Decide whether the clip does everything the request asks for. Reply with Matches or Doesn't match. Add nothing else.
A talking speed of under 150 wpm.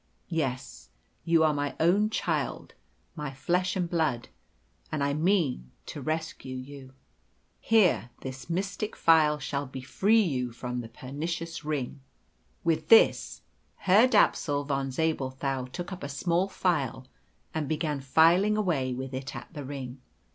Matches